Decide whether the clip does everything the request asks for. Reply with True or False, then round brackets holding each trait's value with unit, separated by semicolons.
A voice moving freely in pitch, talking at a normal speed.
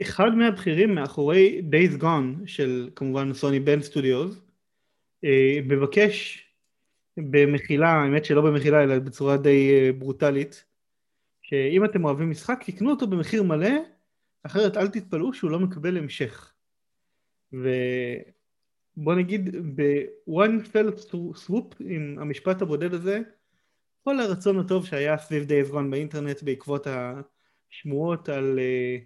True (5.7 semitones; 110 wpm)